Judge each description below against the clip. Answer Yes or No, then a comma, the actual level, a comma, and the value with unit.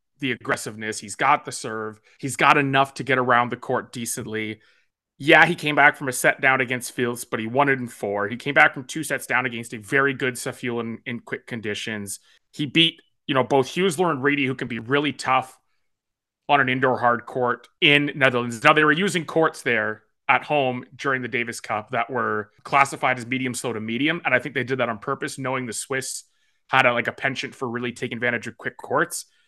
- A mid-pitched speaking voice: No, low, 130 Hz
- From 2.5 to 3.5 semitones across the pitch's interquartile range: Yes, average, 2.8 semitones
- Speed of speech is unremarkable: No, fast, 225 wpm